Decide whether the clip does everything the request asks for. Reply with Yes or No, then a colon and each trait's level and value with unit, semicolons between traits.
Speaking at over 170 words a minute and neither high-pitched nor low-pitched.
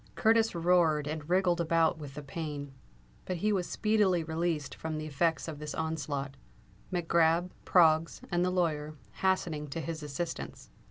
No: average, 160 wpm; medium, 165 Hz